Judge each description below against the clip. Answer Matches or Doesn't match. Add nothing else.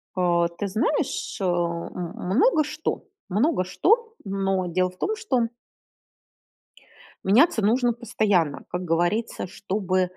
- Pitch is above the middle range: Matches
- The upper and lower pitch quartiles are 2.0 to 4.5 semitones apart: Doesn't match